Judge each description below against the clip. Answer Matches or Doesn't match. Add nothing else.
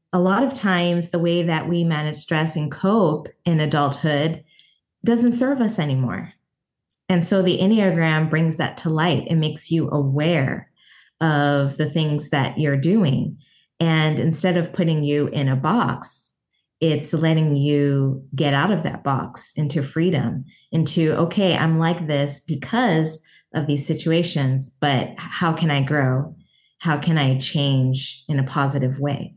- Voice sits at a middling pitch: Matches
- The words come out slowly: Doesn't match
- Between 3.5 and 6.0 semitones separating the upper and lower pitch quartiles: Doesn't match